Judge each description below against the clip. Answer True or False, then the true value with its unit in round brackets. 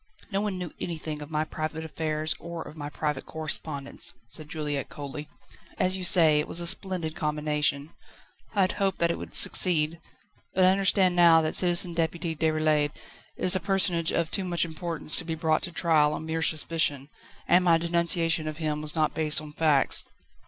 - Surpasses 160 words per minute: True (190 wpm)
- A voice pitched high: False (160 Hz)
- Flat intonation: True (2.2 semitones)